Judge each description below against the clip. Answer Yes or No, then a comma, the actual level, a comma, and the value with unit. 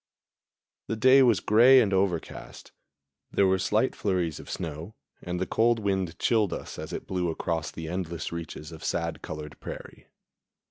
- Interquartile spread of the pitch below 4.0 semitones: No, average, 4.4 semitones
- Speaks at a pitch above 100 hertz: No, very low, 95 Hz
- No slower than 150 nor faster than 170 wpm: Yes, average, 160 wpm